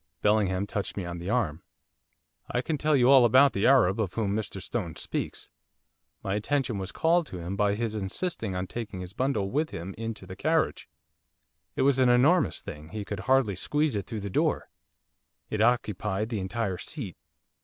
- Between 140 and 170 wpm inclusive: No, average, 185 wpm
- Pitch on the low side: Yes, low, 105 Hz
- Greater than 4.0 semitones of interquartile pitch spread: Yes, average, 5.1 semitones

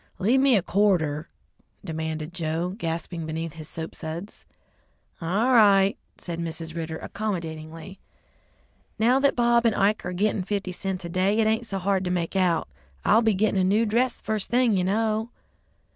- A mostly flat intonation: No, average, 4.6 semitones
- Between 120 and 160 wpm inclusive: No, average, 170 wpm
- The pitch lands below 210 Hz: Yes, high, 190 Hz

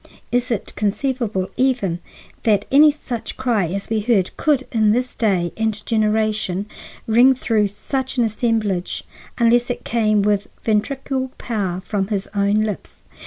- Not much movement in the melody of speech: No, average, 3.2 semitones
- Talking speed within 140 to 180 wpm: Yes, average, 145 wpm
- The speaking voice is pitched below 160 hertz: No, high, 220 Hz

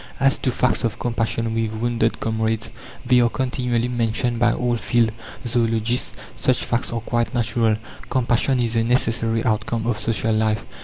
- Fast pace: No, average, 160 wpm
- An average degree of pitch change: No, narrow, 1.3 semitones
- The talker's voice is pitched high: No, low, 115 Hz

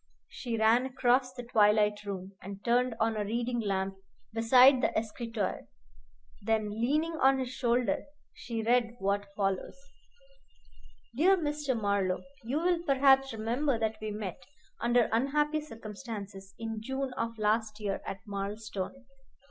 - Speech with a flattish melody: No, average, 3.6 semitones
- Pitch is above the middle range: Yes, high, 230 Hz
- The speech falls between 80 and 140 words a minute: Yes, slow, 135 wpm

